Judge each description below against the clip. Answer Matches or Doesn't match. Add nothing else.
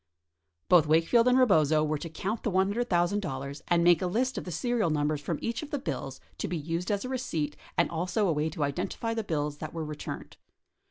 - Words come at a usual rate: Doesn't match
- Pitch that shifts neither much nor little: Doesn't match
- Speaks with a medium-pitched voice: Matches